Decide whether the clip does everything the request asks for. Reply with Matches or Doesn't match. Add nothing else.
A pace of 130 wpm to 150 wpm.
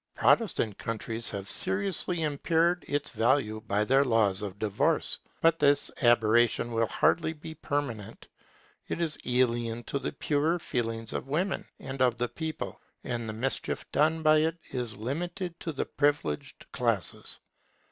Matches